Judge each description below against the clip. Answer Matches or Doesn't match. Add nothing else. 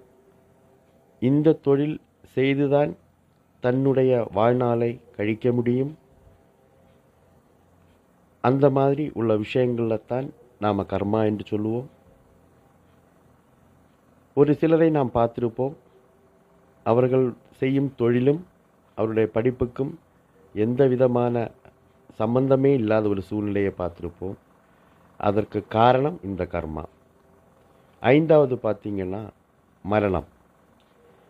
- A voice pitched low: Matches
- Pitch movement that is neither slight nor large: Matches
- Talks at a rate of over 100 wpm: Doesn't match